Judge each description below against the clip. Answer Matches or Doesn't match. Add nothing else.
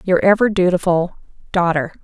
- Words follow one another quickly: Doesn't match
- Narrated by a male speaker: Doesn't match